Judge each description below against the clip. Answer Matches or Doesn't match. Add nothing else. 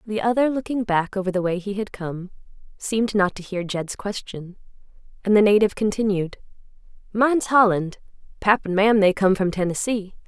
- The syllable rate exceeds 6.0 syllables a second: Doesn't match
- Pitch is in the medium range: Doesn't match